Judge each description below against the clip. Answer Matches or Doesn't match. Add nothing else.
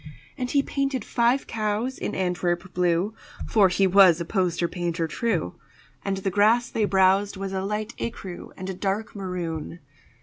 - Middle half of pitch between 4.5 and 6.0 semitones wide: Doesn't match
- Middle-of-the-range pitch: Doesn't match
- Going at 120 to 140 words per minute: Doesn't match